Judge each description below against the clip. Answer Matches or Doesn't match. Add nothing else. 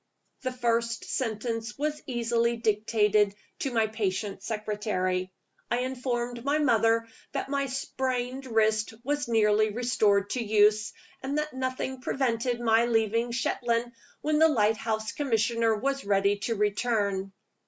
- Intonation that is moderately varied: Matches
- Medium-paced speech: Doesn't match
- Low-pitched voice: Doesn't match